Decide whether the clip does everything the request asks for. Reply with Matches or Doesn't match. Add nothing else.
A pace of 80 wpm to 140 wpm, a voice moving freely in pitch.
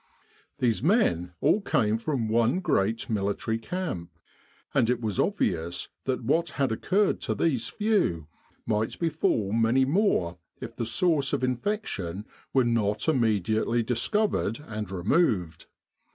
Matches